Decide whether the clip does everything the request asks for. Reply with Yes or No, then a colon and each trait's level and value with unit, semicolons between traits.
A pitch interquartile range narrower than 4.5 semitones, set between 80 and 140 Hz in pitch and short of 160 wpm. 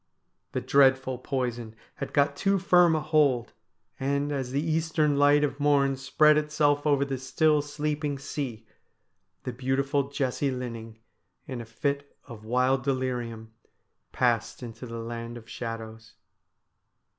Yes: average, 3.3 semitones; low, 135 Hz; slow, 135 wpm